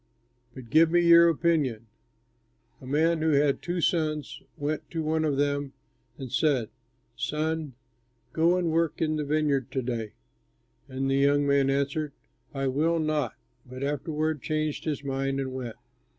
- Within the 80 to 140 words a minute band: No, average, 155 wpm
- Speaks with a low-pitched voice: No, medium, 145 Hz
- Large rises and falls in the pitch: No, average, 2.7 semitones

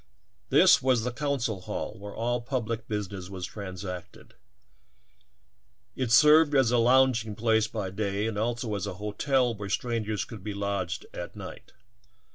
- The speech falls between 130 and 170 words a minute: Yes, average, 155 wpm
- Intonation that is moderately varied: Yes, average, 3.3 semitones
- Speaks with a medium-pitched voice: No, low, 110 Hz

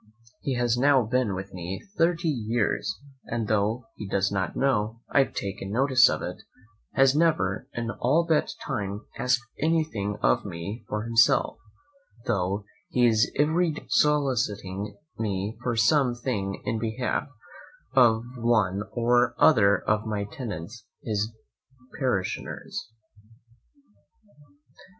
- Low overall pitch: Yes, low, 115 Hz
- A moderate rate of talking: No, slow, 125 wpm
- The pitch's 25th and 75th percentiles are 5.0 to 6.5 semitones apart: No, average, 4.2 semitones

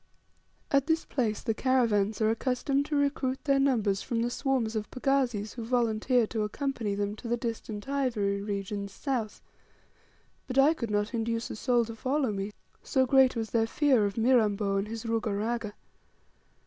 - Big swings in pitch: No, average, 3.7 semitones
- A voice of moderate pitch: No, high, 230 Hz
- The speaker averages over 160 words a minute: Yes, average, 175 wpm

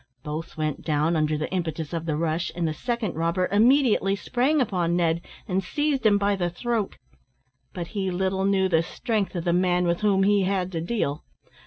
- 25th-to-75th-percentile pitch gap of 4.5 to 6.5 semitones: No, average, 3.5 semitones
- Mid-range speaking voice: Yes, medium, 180 Hz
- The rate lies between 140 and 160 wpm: No, average, 195 wpm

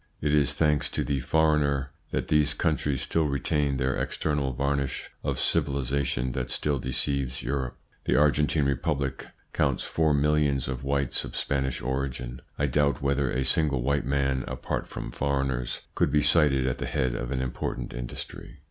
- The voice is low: Yes, very low, 70 Hz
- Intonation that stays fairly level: Yes, narrow, 1.8 semitones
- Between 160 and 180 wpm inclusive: Yes, average, 165 wpm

